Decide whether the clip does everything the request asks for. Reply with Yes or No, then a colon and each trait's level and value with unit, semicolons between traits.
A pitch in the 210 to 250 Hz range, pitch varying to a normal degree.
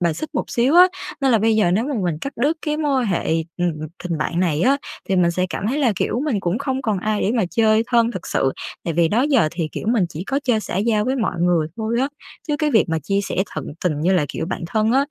No: high, 215 Hz; wide, 6.5 semitones